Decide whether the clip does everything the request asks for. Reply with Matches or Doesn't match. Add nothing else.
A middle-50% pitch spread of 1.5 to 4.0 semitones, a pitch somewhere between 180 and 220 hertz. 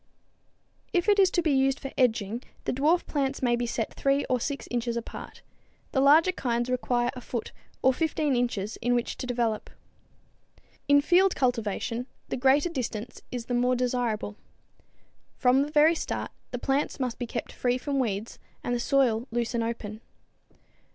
Doesn't match